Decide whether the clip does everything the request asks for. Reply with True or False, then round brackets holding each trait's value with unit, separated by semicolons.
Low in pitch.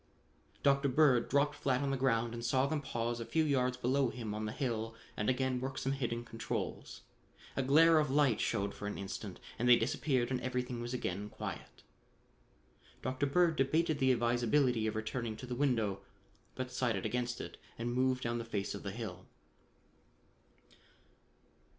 True (125 Hz)